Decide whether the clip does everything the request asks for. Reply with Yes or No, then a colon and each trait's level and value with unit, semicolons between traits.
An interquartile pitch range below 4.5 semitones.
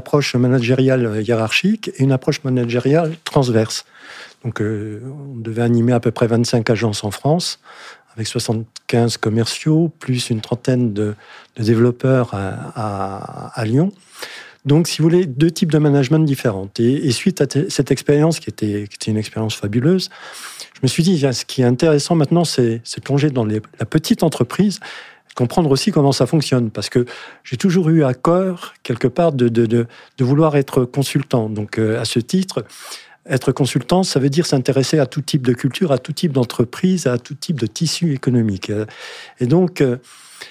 No: average, 4.9 semitones